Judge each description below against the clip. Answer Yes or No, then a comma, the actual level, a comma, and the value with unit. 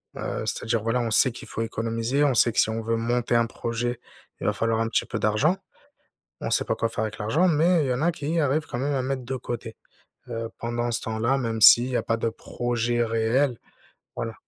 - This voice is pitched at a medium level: No, low, 120 Hz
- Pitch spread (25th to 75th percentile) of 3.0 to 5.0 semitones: No, narrow, 2.5 semitones